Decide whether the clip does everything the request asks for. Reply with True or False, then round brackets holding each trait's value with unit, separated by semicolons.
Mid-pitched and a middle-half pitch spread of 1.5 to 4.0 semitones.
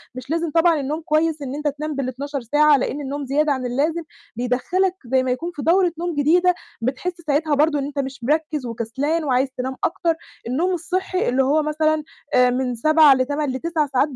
False (295 Hz; 3.5 semitones)